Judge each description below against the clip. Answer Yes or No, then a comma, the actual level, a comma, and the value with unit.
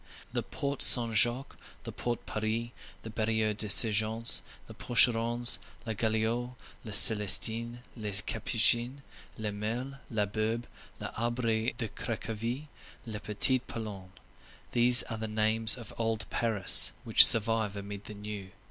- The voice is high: No, low, 110 Hz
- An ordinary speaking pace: No, slow, 130 wpm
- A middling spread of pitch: No, narrow, 1.8 semitones